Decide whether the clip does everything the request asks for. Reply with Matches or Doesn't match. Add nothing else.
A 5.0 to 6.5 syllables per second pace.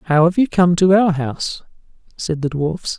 Doesn't match